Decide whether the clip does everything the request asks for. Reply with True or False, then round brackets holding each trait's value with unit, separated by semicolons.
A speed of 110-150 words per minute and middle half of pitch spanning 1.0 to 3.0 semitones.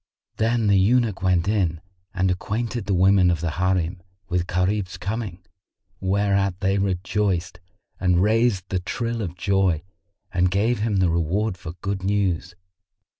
True (145 wpm; 2.4 semitones)